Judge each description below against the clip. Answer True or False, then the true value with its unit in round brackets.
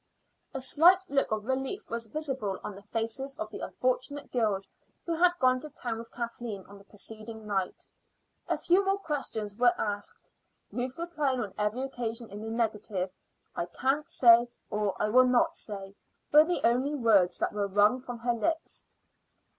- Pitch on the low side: False (235 Hz)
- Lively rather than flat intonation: False (4.6 semitones)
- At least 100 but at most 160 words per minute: False (175 wpm)